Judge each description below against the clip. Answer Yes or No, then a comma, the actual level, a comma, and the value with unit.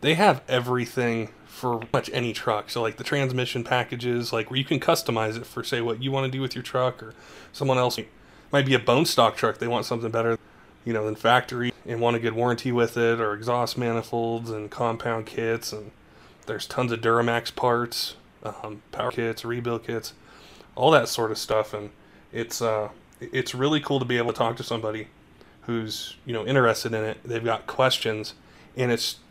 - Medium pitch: No, low, 115 Hz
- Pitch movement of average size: No, narrow, 1.8 semitones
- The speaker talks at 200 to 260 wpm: Yes, fast, 205 wpm